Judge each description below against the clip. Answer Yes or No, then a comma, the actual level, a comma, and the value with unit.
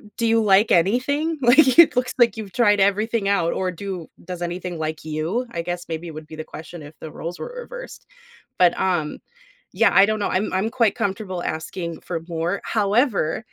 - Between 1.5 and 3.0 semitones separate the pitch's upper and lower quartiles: No, average, 5.1 semitones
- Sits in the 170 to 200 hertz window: Yes, high, 190 Hz